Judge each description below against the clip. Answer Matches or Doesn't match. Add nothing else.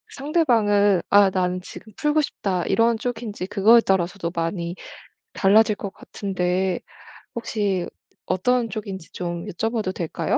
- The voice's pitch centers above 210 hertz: Doesn't match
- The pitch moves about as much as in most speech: Matches